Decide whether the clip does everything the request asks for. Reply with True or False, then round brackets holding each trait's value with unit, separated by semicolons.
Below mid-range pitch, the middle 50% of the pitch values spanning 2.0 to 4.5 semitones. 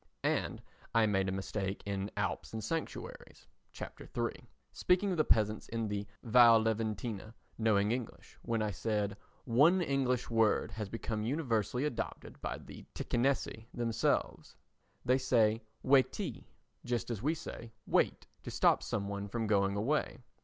True (115 Hz; 3.3 semitones)